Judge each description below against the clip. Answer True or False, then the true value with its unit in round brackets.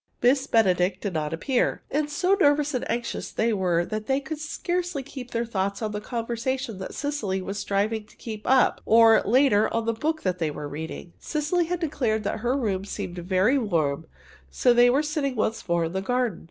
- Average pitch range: False (6.1 semitones)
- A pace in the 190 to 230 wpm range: True (200 wpm)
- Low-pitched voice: False (230 Hz)